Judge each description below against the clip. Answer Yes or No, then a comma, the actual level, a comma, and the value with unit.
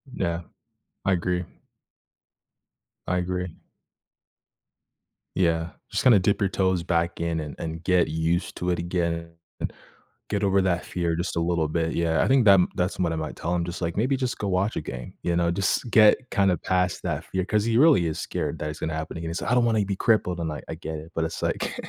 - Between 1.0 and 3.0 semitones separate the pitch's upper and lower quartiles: Yes, narrow, 2.6 semitones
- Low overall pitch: Yes, very low, 90 Hz